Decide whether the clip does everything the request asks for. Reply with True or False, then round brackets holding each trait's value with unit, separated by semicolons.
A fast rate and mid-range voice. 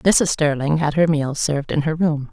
True (235 wpm; 155 Hz)